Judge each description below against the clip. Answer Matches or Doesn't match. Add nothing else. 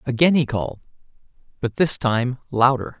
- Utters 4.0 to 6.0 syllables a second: Matches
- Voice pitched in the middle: Doesn't match